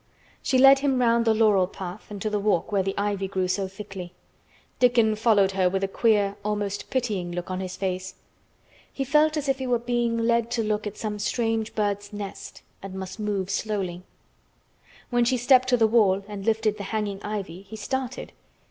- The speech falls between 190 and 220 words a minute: Yes, average, 195 wpm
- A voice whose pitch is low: No, high, 210 Hz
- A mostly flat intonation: No, average, 3.2 semitones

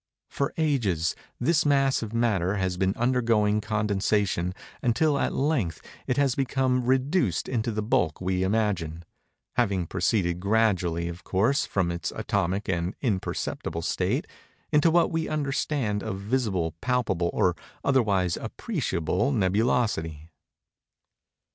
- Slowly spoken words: Yes, slow, 125 wpm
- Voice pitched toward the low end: Yes, low, 105 Hz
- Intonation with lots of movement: Yes, wide, 6.1 semitones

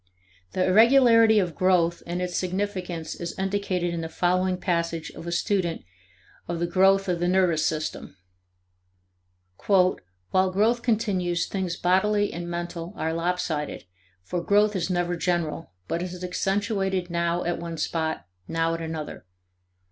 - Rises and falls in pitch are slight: Yes, narrow, 2.2 semitones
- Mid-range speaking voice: Yes, medium, 180 Hz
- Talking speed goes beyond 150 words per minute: No, average, 140 wpm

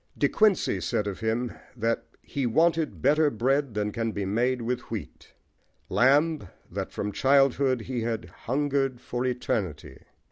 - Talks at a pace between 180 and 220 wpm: No, average, 145 wpm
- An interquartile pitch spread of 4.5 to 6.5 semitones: No, average, 3.8 semitones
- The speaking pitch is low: Yes, low, 125 Hz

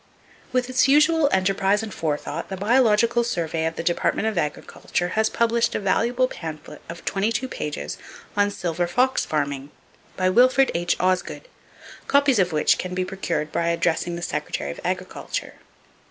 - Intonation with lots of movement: Yes, wide, 5.8 semitones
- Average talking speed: Yes, average, 155 wpm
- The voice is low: No, high, 190 Hz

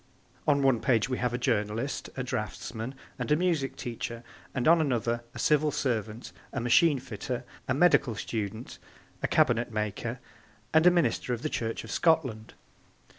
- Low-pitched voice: Yes, low, 125 Hz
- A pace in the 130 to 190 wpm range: Yes, average, 165 wpm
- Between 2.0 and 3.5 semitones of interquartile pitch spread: No, average, 4.1 semitones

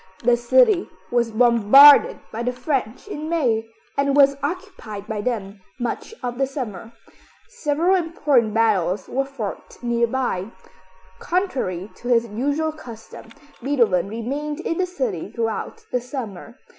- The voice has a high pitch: Yes, high, 245 Hz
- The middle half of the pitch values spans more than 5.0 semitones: No, average, 4.6 semitones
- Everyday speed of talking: No, slow, 130 wpm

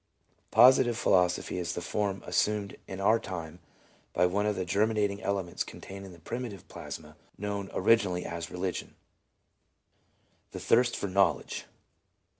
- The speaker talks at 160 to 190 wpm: No, slow, 135 wpm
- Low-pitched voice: Yes, very low, 95 Hz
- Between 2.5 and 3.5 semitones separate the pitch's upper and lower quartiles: Yes, average, 2.8 semitones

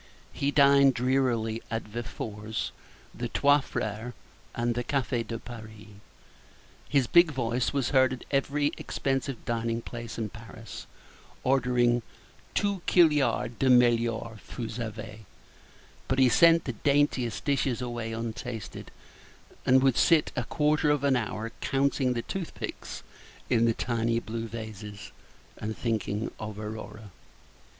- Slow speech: Yes, slow, 130 wpm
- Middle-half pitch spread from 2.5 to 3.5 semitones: Yes, average, 3.2 semitones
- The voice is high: No, low, 120 Hz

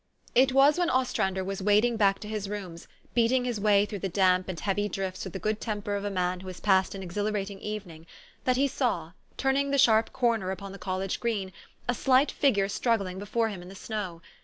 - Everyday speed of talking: No, fast, 220 wpm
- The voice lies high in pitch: Yes, high, 205 Hz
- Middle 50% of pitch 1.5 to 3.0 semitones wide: No, average, 3.6 semitones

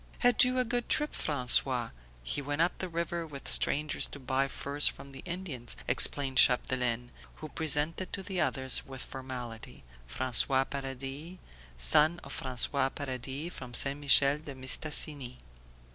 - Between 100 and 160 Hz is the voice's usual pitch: Yes, medium, 140 Hz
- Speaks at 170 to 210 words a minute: No, average, 145 wpm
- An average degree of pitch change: Yes, average, 3.4 semitones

